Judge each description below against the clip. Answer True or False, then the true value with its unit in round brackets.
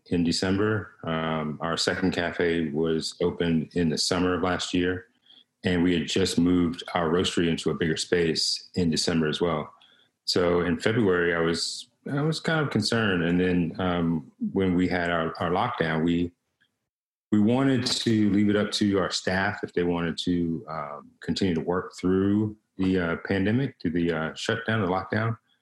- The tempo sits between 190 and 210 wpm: False (180 wpm)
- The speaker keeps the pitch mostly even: False (3.8 semitones)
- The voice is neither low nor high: False (90 Hz)